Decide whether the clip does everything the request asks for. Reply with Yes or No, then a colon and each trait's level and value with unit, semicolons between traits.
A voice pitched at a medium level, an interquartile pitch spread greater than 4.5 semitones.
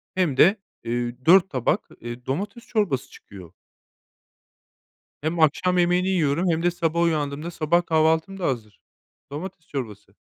Yes: medium, 160 Hz; average, 4.9 semitones